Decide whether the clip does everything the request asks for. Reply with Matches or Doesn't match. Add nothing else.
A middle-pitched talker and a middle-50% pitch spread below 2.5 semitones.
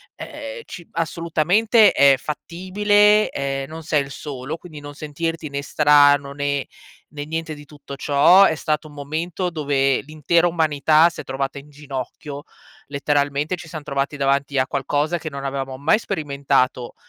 Doesn't match